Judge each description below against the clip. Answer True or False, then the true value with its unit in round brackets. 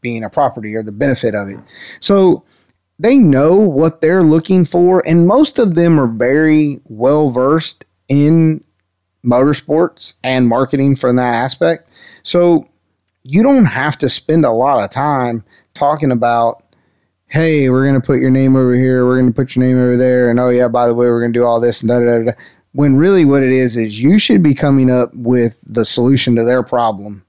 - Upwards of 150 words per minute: True (200 wpm)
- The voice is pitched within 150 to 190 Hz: False (130 Hz)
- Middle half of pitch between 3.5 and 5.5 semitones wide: True (4.0 semitones)